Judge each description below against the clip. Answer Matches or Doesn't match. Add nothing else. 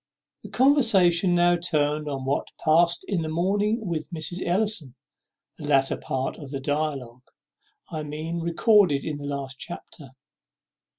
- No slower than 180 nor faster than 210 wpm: Doesn't match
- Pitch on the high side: Doesn't match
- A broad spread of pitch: Doesn't match